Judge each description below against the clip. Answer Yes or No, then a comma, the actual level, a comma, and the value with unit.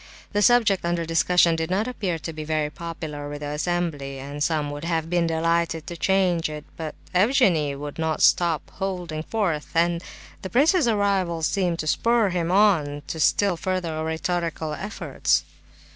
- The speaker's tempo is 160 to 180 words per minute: Yes, average, 165 wpm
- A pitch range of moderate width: Yes, average, 3.2 semitones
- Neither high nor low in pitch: Yes, medium, 170 Hz